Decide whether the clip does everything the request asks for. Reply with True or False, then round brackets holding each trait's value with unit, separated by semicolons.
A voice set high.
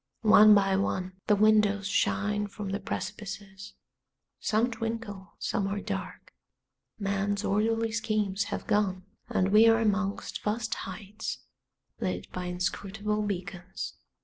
True (205 Hz)